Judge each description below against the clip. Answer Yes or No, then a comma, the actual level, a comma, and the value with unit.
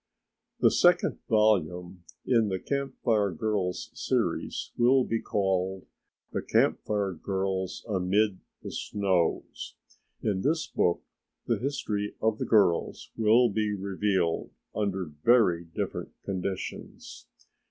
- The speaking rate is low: Yes, slow, 115 wpm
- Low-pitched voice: Yes, low, 100 Hz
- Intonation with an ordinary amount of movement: Yes, average, 3.0 semitones